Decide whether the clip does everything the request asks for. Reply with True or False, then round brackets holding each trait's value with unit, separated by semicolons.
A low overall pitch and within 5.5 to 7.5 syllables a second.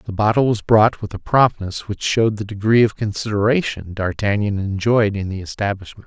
False (105 Hz; 5.3 syllables/s)